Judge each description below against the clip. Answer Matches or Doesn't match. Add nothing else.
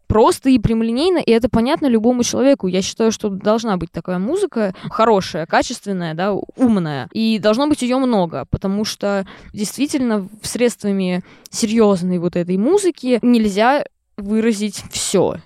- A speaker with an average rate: Matches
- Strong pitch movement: Doesn't match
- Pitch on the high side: Matches